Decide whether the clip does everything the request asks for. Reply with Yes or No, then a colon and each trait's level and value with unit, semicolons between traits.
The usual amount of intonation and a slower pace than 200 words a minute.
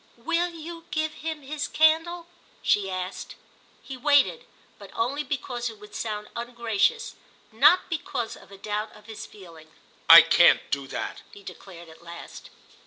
No: wide, 7.4 semitones; average, 155 wpm